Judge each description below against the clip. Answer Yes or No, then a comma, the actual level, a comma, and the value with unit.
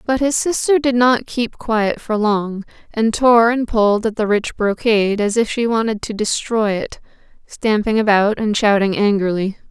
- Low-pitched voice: No, high, 220 Hz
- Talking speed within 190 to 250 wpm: No, average, 180 wpm